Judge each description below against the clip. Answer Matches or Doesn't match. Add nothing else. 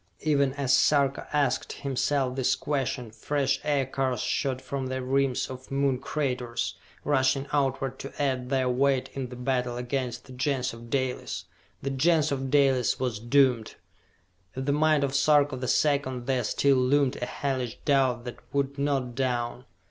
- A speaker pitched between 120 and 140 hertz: Matches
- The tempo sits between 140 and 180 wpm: Matches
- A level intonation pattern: Matches